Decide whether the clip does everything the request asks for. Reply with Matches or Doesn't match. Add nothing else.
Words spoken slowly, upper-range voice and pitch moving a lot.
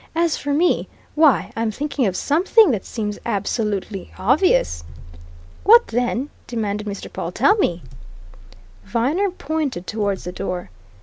Matches